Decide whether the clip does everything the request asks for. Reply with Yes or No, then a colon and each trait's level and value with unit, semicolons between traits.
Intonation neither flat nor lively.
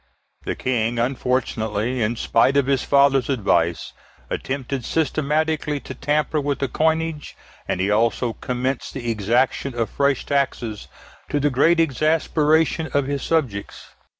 Yes: average, 3.8 semitones